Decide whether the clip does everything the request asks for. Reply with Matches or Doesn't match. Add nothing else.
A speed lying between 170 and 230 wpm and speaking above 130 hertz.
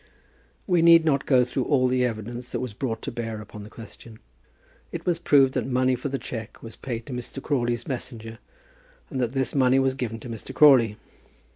Doesn't match